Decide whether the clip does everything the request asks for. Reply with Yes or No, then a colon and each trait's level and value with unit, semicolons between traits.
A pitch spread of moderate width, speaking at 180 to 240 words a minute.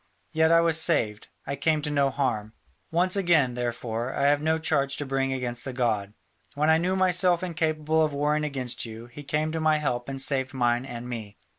Yes: average, 4.4 semitones; fast, 205 wpm